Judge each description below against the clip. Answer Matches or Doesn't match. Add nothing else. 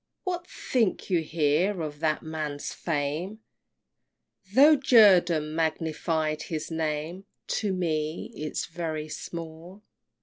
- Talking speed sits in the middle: Doesn't match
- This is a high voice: Doesn't match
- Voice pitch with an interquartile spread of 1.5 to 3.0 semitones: Doesn't match